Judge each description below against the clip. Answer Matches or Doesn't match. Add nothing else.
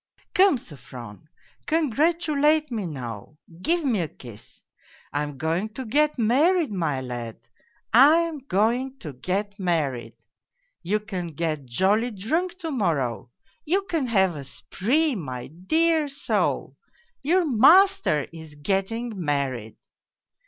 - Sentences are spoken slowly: Matches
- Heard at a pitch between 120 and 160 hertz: Doesn't match